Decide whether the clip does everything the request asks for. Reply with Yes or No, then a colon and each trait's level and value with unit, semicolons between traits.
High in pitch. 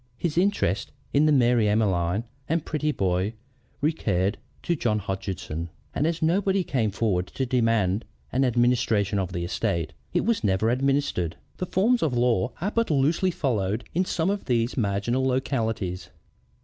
No: low, 120 Hz